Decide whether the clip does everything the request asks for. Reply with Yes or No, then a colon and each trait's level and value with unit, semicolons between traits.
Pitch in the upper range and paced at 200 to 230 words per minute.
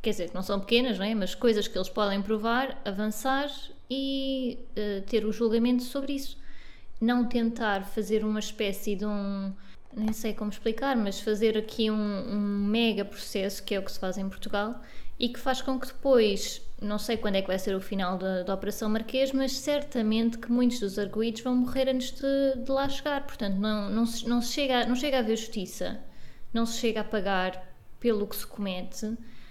Yes: high, 220 Hz; fast, 205 wpm